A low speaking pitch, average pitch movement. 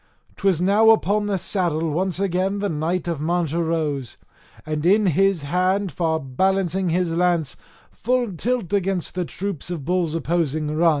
No: medium, 175 Hz; average, 3.2 semitones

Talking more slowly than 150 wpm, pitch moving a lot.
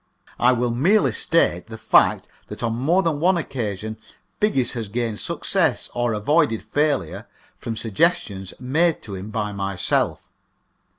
Yes: average, 140 wpm; wide, 6.6 semitones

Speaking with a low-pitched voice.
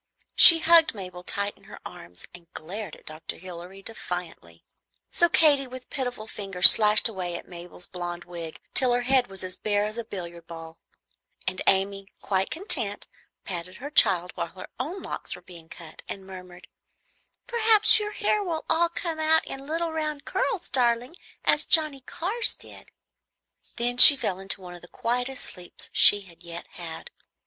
No: high, 205 Hz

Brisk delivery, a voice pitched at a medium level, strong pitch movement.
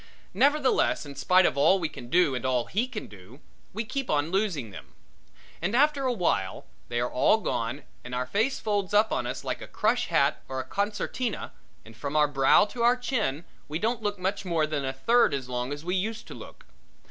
Yes: fast, 215 wpm; medium, 175 Hz; wide, 8.6 semitones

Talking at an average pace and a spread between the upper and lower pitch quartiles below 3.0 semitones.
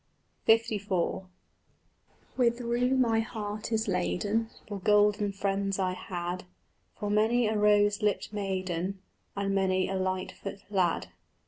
No: slow, 120 wpm; narrow, 2.5 semitones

